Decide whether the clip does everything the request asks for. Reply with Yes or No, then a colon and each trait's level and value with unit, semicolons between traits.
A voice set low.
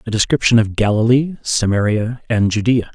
Yes: low, 115 Hz